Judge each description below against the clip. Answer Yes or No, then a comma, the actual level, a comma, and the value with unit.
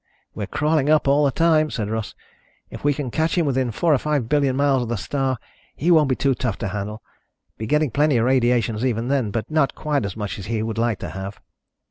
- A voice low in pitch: Yes, low, 130 Hz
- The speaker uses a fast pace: Yes, fast, 235 wpm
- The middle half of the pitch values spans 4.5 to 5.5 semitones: Yes, average, 4.8 semitones